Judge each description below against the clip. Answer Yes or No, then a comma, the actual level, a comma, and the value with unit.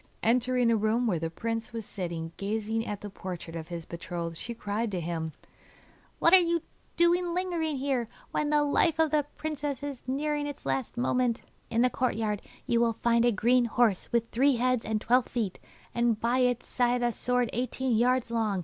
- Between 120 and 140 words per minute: No, average, 195 wpm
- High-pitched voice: Yes, high, 235 Hz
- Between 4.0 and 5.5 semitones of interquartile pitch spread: No, average, 3.4 semitones